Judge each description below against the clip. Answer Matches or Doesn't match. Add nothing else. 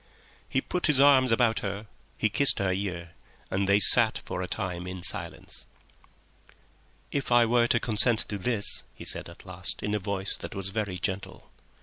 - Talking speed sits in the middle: Matches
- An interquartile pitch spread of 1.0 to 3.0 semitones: Doesn't match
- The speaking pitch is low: Matches